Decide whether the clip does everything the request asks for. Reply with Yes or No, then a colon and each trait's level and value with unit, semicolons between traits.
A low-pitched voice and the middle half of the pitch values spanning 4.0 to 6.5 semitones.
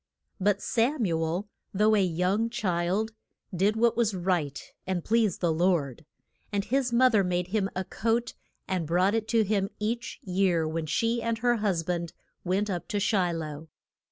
No: high, 195 Hz; average, 4.3 semitones